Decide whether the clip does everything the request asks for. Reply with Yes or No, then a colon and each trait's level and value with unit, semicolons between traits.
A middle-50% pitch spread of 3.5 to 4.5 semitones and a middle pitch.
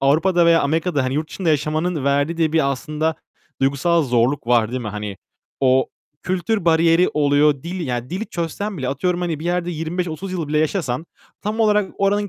Yes: average, 4.2 semitones; medium, 160 Hz